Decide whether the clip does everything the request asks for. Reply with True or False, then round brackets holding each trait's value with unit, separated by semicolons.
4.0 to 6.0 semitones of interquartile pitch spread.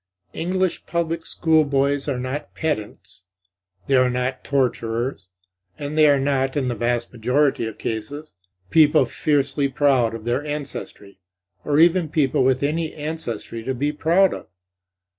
False (3.5 semitones)